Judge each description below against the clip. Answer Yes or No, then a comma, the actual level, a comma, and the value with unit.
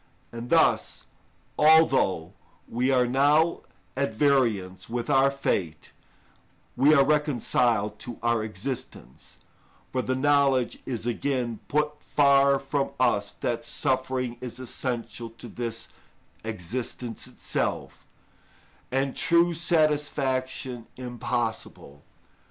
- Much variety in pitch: No, average, 3.2 semitones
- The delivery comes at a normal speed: No, slow, 100 wpm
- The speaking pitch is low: Yes, low, 130 Hz